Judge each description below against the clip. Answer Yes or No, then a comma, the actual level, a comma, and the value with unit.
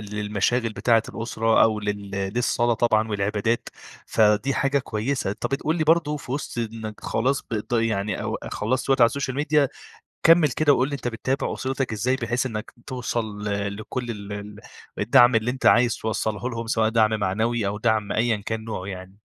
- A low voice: Yes, low, 115 Hz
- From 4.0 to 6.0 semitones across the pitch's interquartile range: No, average, 3.4 semitones